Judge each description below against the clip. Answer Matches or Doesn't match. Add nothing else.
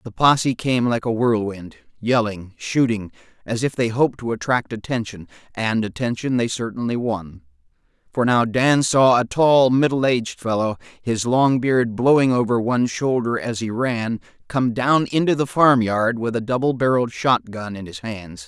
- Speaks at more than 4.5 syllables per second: Matches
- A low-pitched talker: Matches